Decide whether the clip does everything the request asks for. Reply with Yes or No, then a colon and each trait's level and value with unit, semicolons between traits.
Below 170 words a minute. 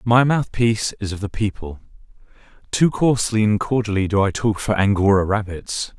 Yes: average, 150 wpm